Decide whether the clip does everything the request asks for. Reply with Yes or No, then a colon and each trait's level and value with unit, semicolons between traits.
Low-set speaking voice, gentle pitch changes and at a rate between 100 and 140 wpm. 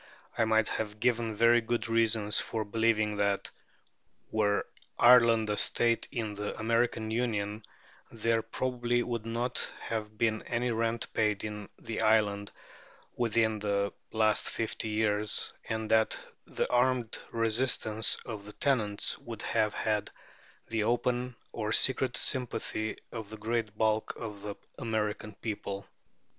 Yes: low, 110 Hz; narrow, 1.6 semitones; slow, 135 wpm